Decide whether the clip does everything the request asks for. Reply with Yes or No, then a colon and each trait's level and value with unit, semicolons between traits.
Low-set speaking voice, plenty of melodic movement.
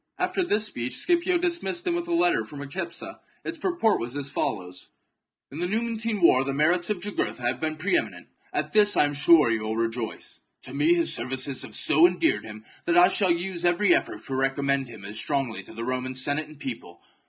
No: medium, 155 Hz; wide, 8.3 semitones